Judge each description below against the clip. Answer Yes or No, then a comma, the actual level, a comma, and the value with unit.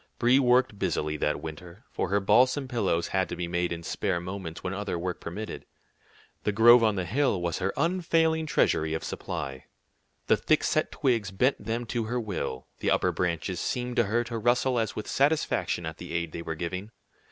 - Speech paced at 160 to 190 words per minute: No, average, 200 wpm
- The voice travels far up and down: Yes, wide, 6.0 semitones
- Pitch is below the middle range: Yes, low, 100 Hz